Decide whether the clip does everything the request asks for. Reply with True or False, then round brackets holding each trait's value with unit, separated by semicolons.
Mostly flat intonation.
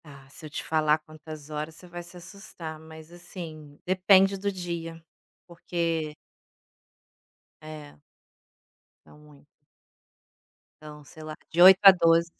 True (2.3 semitones)